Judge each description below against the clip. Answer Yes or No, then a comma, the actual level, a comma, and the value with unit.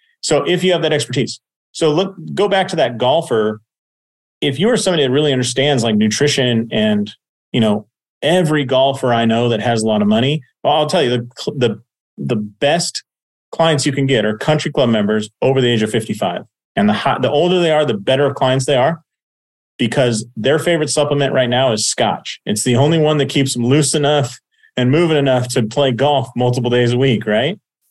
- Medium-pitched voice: No, low, 130 Hz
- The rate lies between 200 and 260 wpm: Yes, fast, 205 wpm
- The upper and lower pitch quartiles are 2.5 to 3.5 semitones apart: No, average, 4.5 semitones